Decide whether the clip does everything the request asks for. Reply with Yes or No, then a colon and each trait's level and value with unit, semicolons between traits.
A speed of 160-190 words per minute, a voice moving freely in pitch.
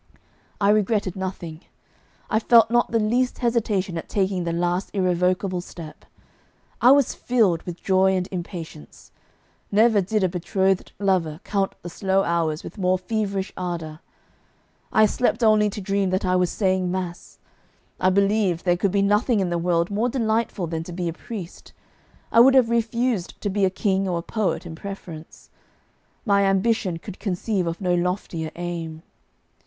No: average, 165 wpm; average, 3.2 semitones